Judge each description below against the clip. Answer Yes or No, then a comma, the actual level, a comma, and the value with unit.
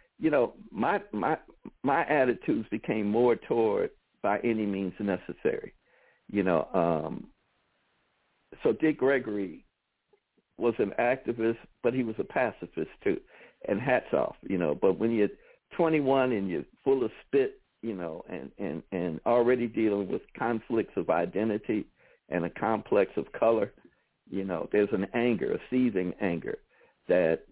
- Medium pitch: No, low, 115 Hz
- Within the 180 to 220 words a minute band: No, average, 145 wpm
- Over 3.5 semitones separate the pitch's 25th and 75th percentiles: Yes, wide, 5.6 semitones